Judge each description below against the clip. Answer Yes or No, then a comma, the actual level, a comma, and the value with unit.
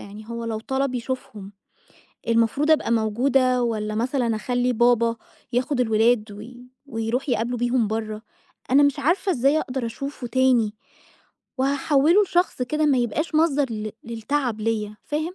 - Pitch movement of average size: Yes, average, 3.6 semitones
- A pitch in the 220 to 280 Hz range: Yes, high, 245 Hz